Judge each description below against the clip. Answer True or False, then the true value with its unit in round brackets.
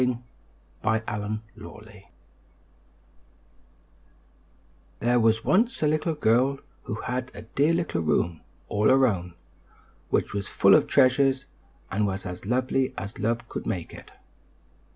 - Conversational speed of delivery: False (130 wpm)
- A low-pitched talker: True (115 Hz)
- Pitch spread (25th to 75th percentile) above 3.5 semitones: True (4.2 semitones)